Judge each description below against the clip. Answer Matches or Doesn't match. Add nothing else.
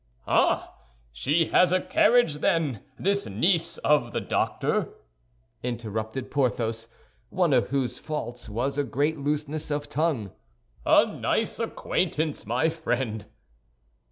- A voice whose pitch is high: Doesn't match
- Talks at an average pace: Doesn't match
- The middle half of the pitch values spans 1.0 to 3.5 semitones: Doesn't match